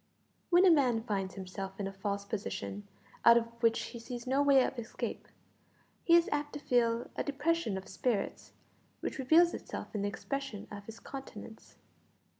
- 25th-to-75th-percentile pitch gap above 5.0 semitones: Yes, wide, 5.4 semitones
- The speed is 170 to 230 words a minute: Yes, average, 175 wpm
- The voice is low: No, high, 235 Hz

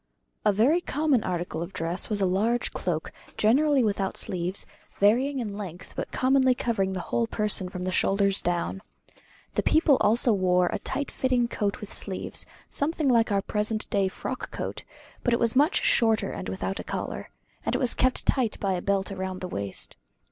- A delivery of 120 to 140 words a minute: No, average, 185 wpm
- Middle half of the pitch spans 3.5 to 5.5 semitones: Yes, average, 4.7 semitones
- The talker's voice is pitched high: Yes, high, 210 Hz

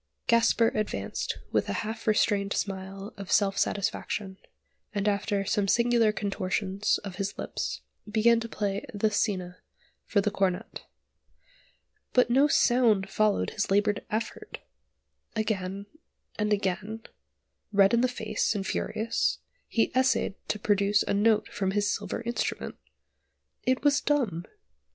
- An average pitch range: No, narrow, 2.3 semitones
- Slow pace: Yes, slow, 130 wpm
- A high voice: Yes, high, 210 Hz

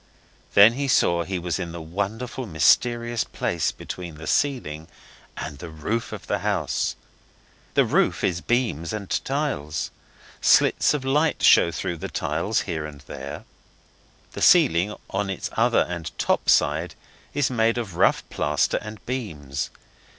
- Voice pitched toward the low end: Yes, very low, 95 Hz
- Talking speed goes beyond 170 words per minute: No, average, 150 wpm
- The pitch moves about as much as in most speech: No, wide, 6.7 semitones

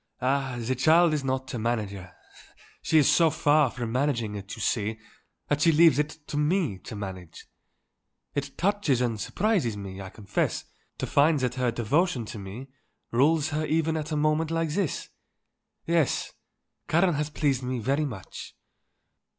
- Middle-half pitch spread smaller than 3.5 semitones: No, average, 5.2 semitones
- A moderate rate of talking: Yes, average, 165 wpm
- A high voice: No, medium, 140 Hz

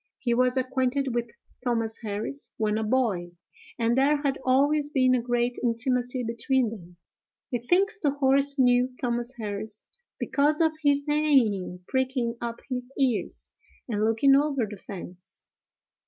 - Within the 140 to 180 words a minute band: Yes, average, 145 wpm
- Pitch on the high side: Yes, very high, 250 Hz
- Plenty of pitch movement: No, average, 3.2 semitones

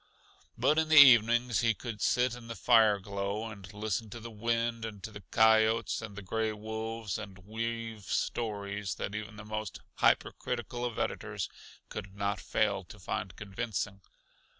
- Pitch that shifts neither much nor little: No, narrow, 2.2 semitones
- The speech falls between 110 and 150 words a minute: No, average, 170 wpm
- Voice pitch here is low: Yes, low, 110 Hz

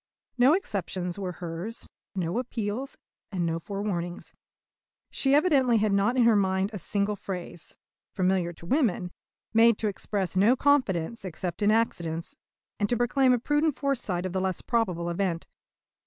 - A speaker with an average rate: Yes, average, 155 wpm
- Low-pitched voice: No, high, 200 Hz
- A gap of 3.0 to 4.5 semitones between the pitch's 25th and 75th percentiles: No, average, 5.0 semitones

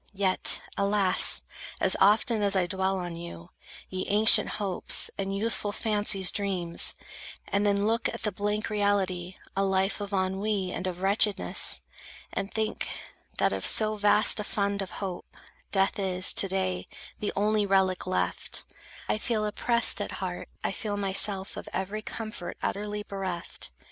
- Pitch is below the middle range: No, high, 200 Hz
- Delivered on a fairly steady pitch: Yes, narrow, 1.7 semitones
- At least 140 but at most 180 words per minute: Yes, average, 155 wpm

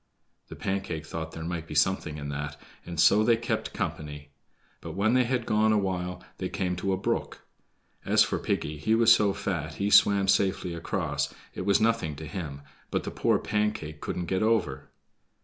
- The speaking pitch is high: No, very low, 95 Hz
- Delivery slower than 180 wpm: No, average, 185 wpm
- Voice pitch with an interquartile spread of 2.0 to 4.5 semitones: No, average, 5.3 semitones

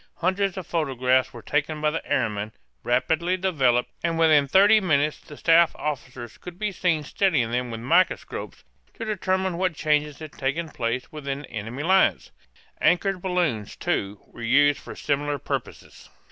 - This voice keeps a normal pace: Yes, average, 160 wpm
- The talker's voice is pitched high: No, medium, 150 Hz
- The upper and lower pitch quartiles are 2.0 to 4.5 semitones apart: No, wide, 5.6 semitones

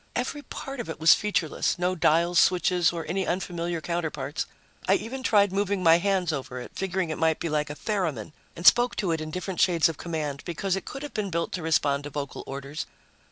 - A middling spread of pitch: Yes, average, 3.7 semitones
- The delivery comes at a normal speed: No, fast, 215 wpm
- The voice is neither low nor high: Yes, medium, 170 Hz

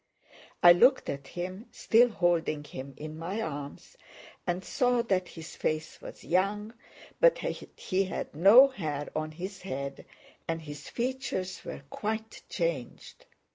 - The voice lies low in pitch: No, medium, 180 Hz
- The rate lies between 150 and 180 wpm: No, average, 140 wpm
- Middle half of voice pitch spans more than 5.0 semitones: Yes, wide, 5.6 semitones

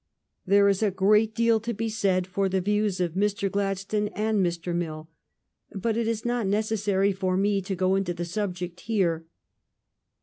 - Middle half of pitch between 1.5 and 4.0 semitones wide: Yes, narrow, 2.5 semitones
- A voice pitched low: No, high, 195 Hz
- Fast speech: No, average, 175 wpm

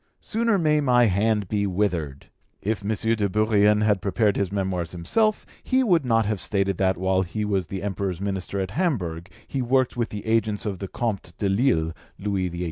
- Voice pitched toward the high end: No, low, 100 Hz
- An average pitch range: Yes, average, 3.3 semitones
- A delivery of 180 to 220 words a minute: Yes, average, 195 wpm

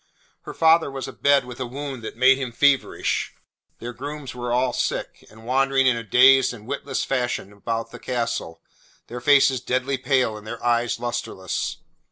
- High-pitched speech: No, low, 125 Hz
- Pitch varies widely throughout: No, narrow, 2.4 semitones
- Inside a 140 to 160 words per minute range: No, average, 175 wpm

